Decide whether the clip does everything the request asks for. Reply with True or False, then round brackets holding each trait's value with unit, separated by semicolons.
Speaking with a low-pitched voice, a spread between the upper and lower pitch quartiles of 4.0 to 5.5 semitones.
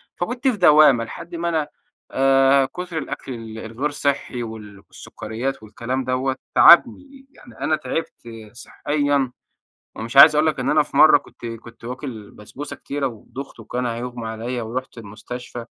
True (130 Hz; 4.3 semitones)